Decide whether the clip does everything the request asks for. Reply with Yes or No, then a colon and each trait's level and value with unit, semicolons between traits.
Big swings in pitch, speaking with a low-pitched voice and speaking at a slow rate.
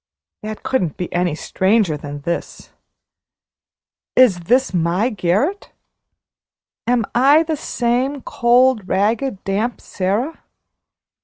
No: wide, 6.1 semitones; high, 220 Hz; slow, 100 wpm